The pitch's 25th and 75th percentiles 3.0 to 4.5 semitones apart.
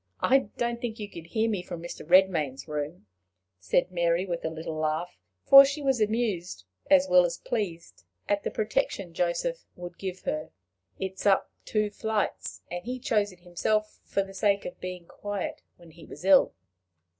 Yes: average, 3.7 semitones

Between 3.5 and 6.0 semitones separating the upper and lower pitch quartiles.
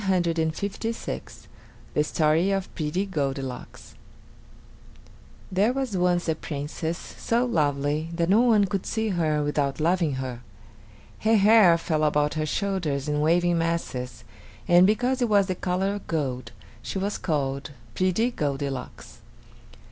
Yes: average, 4.9 semitones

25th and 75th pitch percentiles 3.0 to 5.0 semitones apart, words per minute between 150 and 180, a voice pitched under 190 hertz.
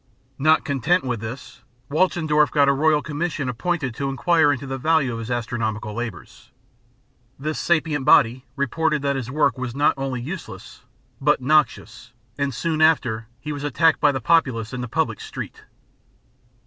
Yes: average, 3.9 semitones; average, 160 wpm; medium, 140 Hz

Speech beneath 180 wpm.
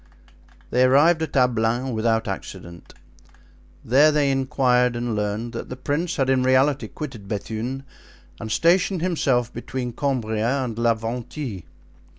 Yes: slow, 135 wpm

